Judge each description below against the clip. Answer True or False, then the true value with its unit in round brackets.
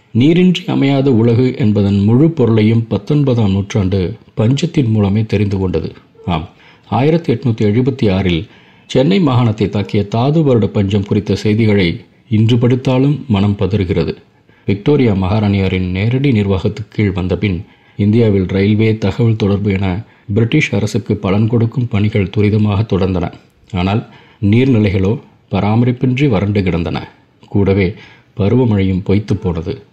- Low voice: True (105 Hz)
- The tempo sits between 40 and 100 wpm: False (110 wpm)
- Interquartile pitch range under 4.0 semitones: True (3.6 semitones)